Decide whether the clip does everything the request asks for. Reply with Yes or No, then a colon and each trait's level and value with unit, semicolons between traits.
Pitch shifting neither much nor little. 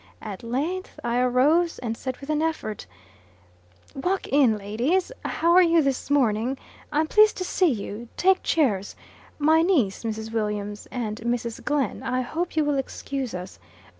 No: wide, 6.2 semitones